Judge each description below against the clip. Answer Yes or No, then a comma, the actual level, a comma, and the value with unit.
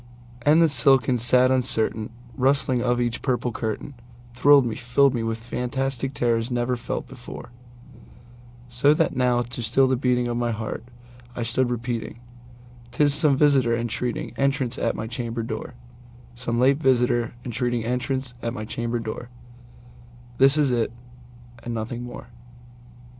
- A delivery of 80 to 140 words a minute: Yes, slow, 135 wpm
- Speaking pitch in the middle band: No, low, 120 Hz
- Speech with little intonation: Yes, narrow, 1.4 semitones